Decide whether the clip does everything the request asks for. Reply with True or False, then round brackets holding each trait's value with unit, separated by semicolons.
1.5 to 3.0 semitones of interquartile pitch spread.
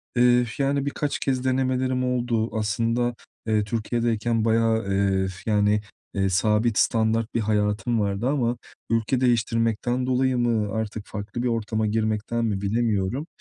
True (2.4 semitones)